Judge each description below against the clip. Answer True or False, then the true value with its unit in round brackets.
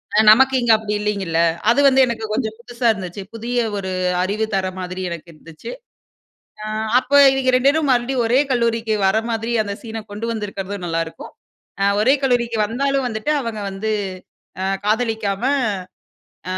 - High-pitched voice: True (220 Hz)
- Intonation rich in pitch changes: False (3.4 semitones)